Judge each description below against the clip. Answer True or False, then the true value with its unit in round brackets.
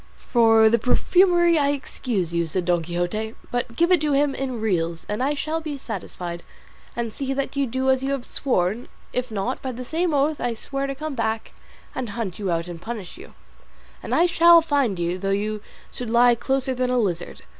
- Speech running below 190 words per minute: False (205 wpm)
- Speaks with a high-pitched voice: True (245 Hz)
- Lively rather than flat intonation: True (5.7 semitones)